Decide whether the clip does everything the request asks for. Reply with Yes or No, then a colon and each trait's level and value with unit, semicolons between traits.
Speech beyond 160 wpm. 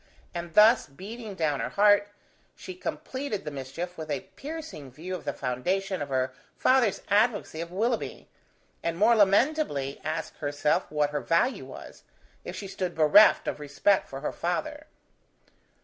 No: average, 155 wpm